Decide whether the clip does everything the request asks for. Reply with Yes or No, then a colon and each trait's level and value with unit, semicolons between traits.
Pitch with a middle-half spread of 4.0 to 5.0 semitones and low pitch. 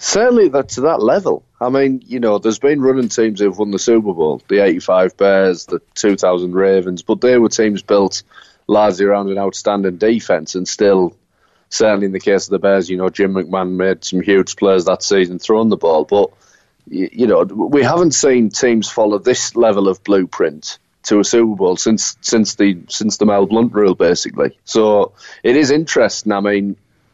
No: average, 2.8 semitones; low, 100 Hz